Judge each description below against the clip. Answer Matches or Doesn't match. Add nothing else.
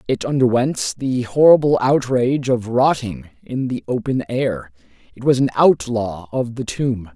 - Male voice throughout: Matches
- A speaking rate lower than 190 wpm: Matches